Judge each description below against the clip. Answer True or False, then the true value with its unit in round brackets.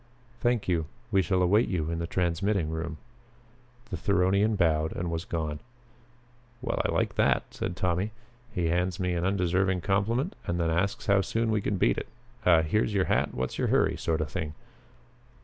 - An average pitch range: True (3.2 semitones)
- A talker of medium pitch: False (90 Hz)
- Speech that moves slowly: False (185 wpm)